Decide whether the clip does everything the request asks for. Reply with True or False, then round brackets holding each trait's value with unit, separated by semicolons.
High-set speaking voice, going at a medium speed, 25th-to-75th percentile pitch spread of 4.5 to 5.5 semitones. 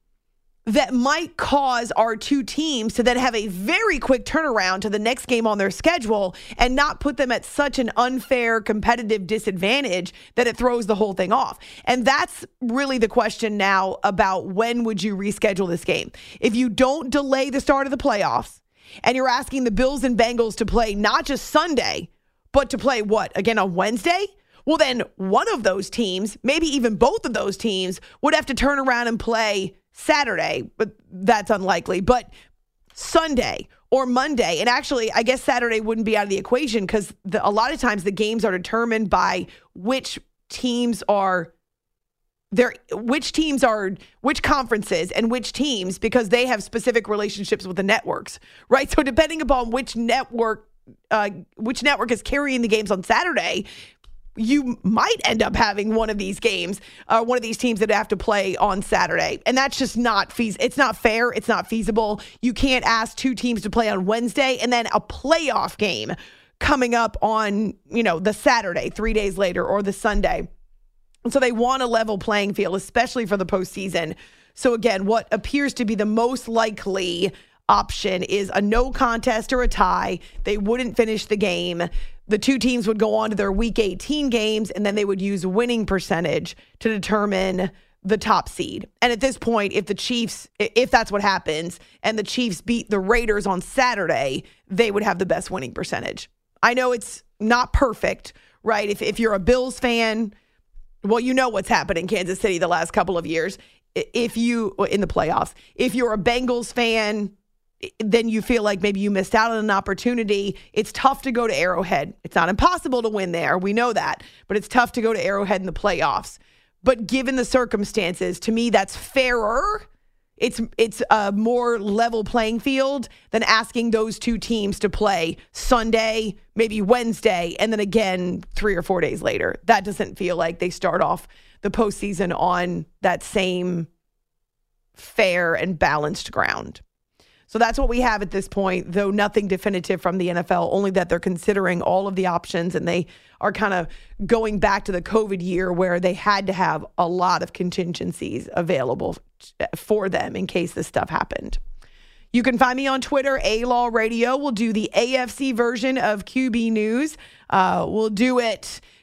False (225 Hz; 185 wpm; 3.7 semitones)